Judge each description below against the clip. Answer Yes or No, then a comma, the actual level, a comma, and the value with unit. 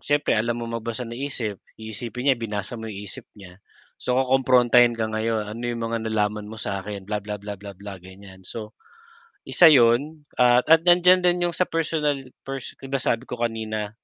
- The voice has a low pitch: Yes, low, 115 Hz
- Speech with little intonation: No, average, 4.1 semitones